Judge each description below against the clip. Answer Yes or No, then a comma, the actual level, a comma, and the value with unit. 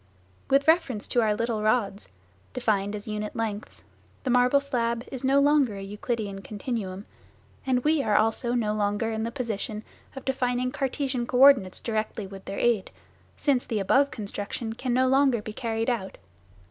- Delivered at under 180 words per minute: Yes, average, 170 wpm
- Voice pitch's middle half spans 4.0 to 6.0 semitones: No, average, 3.5 semitones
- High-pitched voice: Yes, high, 230 Hz